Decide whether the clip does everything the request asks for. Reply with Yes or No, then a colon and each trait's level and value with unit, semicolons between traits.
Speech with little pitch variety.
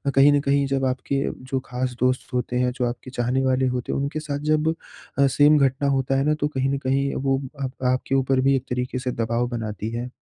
Yes: narrow, 1.6 semitones